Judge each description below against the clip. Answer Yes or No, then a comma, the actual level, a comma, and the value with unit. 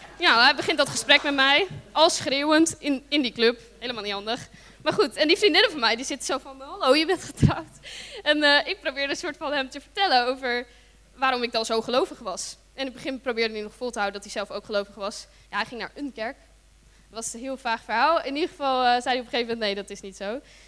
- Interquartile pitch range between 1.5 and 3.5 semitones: No, average, 4.4 semitones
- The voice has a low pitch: No, very high, 255 Hz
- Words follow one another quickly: Yes, fast, 265 wpm